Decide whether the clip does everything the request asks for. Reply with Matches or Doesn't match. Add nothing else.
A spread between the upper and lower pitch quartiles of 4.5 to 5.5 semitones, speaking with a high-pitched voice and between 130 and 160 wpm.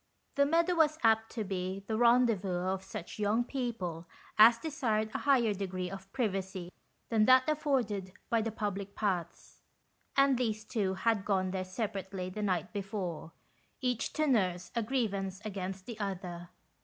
Doesn't match